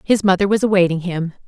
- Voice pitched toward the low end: No, medium, 185 Hz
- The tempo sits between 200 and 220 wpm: Yes, fast, 205 wpm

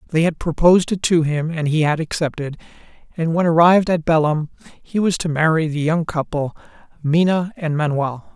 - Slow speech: No, average, 180 wpm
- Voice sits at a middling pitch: Yes, medium, 160 Hz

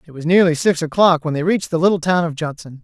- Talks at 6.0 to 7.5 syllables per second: Yes, 6.6 syllables/s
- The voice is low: No, medium, 165 Hz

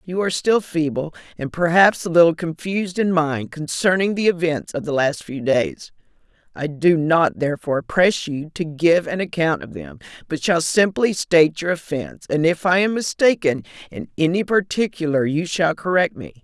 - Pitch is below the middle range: No, medium, 165 Hz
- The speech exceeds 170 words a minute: Yes, average, 180 wpm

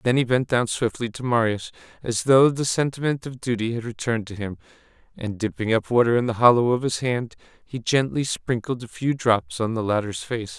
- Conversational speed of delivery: No, fast, 210 wpm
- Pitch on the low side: Yes, low, 120 Hz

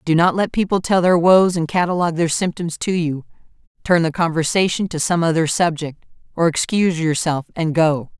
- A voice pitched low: No, medium, 170 Hz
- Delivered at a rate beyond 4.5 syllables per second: Yes, 5.3 syllables/s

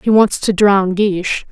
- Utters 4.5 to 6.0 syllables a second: No, 4.1 syllables/s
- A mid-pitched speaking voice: No, high, 200 Hz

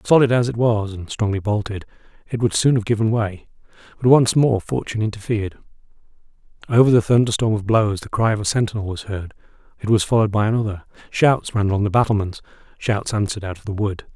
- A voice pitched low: Yes, low, 110 Hz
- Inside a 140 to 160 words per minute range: No, average, 195 wpm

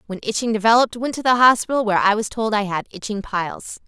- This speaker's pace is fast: Yes, fast, 235 wpm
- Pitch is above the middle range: Yes, high, 220 Hz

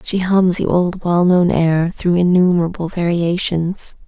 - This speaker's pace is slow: Yes, slow, 130 wpm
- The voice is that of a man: No, female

